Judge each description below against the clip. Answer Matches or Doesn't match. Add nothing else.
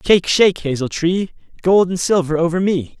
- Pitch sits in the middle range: Matches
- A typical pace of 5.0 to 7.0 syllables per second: Matches